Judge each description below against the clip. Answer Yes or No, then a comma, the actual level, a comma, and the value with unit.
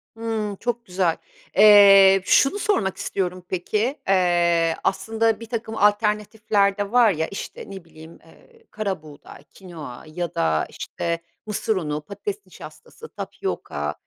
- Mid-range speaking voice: No, high, 195 Hz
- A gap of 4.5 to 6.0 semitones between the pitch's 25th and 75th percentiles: No, average, 3.9 semitones